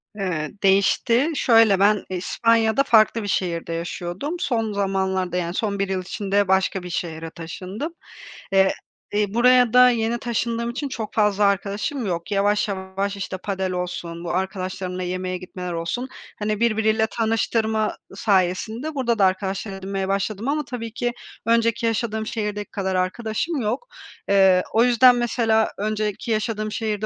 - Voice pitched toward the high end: Yes, high, 205 Hz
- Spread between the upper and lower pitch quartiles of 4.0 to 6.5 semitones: No, average, 3.4 semitones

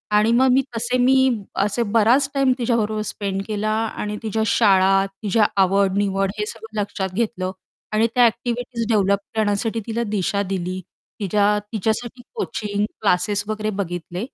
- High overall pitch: Yes, high, 215 Hz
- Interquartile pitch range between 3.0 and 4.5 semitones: No, narrow, 2.6 semitones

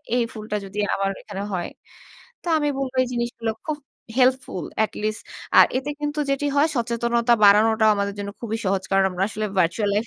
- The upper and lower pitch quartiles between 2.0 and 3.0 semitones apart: No, average, 3.9 semitones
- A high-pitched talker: Yes, high, 220 Hz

